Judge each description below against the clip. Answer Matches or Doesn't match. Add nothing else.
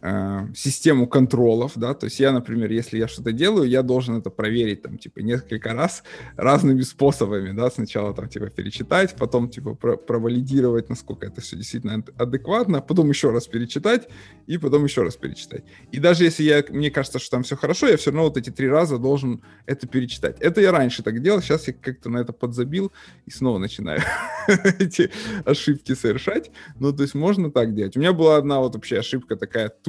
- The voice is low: Matches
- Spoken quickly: Matches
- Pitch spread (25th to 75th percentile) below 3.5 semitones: Doesn't match